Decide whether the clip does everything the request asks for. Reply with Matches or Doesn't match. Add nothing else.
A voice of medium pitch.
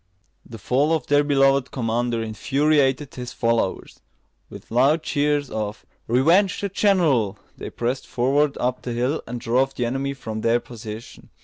Doesn't match